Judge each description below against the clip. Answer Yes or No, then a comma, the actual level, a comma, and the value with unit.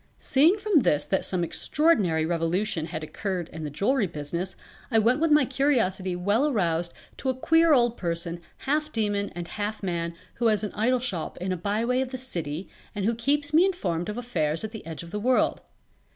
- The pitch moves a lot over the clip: Yes, wide, 7.0 semitones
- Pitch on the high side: Yes, high, 210 Hz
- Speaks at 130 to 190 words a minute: No, average, 200 wpm